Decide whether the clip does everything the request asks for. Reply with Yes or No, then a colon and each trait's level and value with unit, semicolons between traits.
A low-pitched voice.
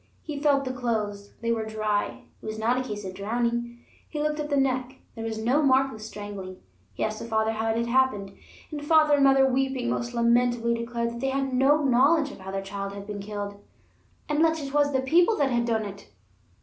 No: high, 240 Hz